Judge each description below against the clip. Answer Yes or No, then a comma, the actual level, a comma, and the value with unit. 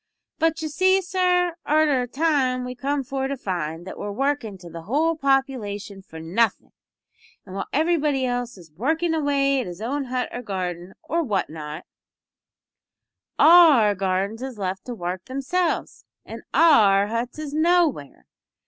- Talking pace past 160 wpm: No, average, 155 wpm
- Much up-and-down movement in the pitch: Yes, wide, 7.6 semitones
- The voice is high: Yes, very high, 255 Hz